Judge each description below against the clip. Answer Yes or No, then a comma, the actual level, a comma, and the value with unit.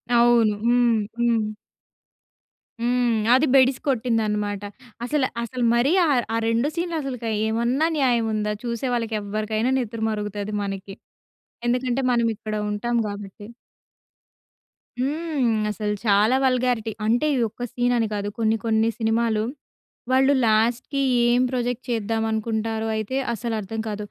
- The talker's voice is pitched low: No, high, 230 Hz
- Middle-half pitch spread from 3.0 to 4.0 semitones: No, narrow, 2.4 semitones